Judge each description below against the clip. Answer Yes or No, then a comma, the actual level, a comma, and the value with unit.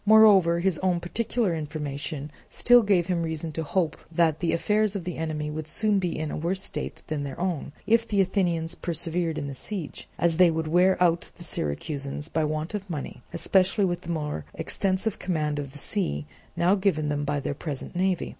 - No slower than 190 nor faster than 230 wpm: Yes, average, 200 wpm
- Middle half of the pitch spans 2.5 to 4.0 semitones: Yes, average, 3.7 semitones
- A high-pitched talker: No, medium, 170 Hz